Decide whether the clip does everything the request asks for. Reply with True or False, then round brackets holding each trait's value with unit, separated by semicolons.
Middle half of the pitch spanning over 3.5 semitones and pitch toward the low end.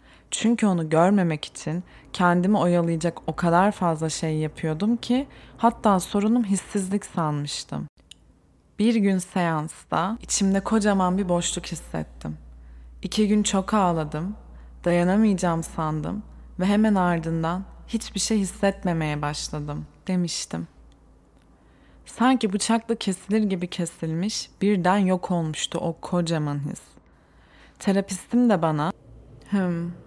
False (4.1 semitones; 180 Hz)